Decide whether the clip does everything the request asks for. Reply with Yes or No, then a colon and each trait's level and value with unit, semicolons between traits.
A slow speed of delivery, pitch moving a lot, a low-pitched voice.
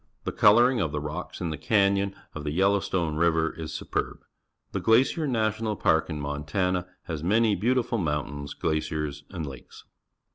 No: average, 155 wpm; wide, 5.7 semitones; very low, 85 Hz